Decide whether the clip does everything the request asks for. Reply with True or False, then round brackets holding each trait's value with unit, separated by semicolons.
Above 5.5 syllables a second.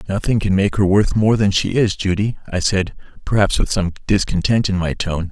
False (5.3 syllables/s)